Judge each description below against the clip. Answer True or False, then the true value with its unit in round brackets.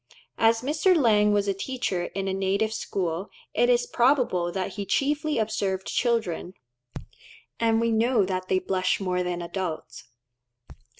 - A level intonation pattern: False (4.1 semitones)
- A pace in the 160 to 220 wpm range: False (145 wpm)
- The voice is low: False (200 Hz)